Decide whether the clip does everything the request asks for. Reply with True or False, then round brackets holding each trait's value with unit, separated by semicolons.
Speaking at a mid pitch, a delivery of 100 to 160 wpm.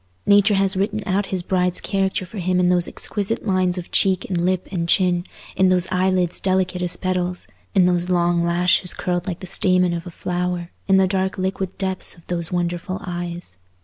False (180 Hz; 195 wpm)